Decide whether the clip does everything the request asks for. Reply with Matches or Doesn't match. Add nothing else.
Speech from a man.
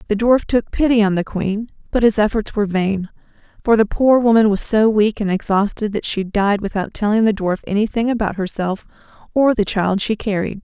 Doesn't match